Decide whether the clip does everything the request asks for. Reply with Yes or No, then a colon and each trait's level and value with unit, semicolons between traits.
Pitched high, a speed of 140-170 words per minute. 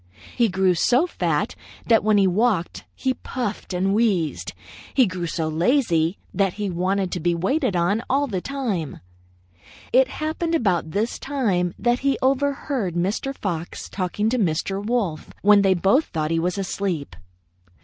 Yes: high, 200 Hz; average, 155 wpm